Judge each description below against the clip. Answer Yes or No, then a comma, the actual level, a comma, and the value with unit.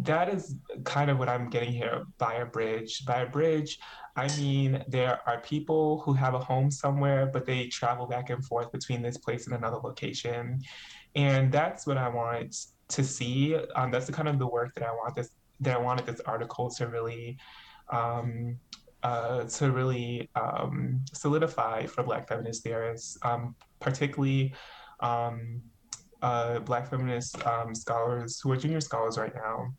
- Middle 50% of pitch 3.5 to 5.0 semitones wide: No, average, 2.7 semitones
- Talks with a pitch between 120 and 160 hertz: Yes, low, 125 Hz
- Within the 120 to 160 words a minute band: No, average, 170 wpm